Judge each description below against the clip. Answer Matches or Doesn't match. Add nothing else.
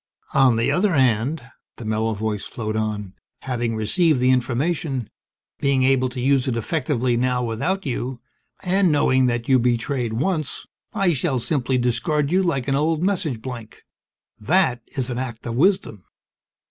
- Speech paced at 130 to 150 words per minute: Doesn't match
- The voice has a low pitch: Matches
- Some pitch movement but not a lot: Matches